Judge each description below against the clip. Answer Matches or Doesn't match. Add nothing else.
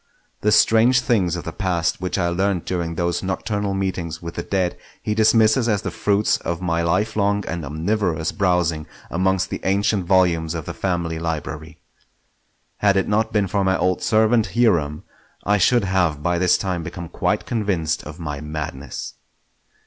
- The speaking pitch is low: Matches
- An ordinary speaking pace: Matches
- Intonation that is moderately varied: Matches